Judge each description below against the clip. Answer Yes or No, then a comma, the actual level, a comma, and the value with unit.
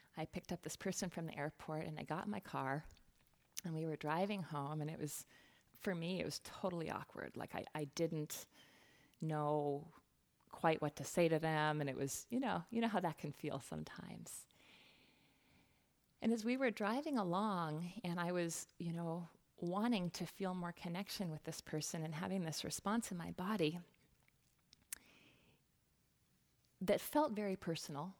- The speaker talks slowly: No, average, 170 wpm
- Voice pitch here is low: No, medium, 170 Hz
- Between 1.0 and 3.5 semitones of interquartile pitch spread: No, average, 3.9 semitones